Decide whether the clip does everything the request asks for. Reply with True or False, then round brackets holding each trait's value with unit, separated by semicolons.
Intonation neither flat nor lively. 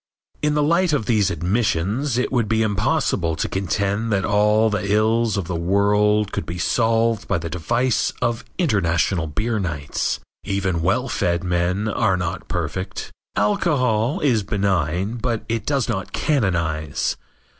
True (4.3 semitones)